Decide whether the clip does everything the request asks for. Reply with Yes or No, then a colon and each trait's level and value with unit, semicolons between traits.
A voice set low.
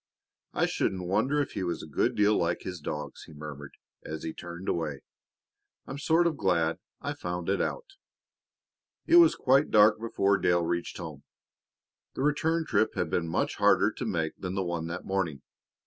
Yes: very low, 90 Hz